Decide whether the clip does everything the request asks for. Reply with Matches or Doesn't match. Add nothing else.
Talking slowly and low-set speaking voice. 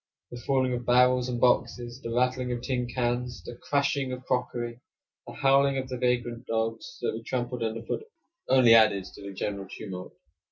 Doesn't match